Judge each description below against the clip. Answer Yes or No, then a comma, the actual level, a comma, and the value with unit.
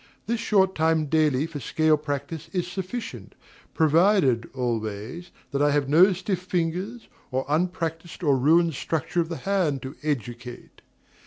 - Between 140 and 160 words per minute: Yes, average, 145 wpm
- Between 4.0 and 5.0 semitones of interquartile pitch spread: Yes, average, 4.3 semitones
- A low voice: No, medium, 160 Hz